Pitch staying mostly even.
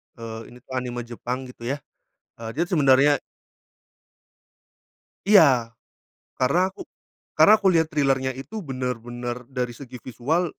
No: average, 3.6 semitones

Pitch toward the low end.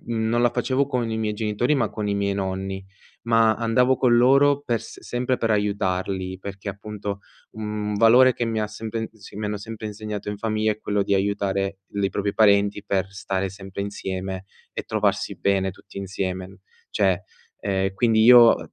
Yes: low, 105 Hz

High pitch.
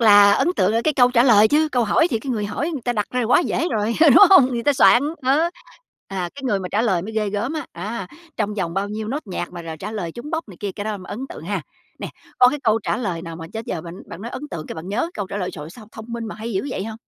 Yes: high, 215 Hz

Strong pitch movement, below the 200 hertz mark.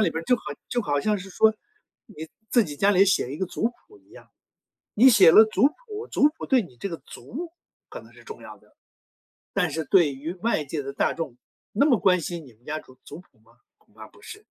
Yes: wide, 7.7 semitones; medium, 185 Hz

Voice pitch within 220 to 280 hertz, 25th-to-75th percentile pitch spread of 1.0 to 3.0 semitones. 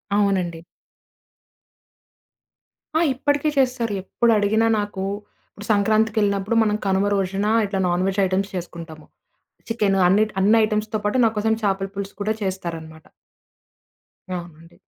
No: high, 200 Hz; narrow, 2.5 semitones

